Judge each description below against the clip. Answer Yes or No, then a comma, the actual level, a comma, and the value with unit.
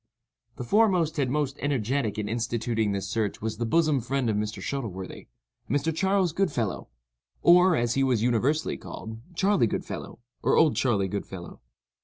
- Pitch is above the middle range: No, low, 125 Hz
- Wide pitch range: Yes, wide, 5.9 semitones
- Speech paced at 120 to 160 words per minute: Yes, average, 155 wpm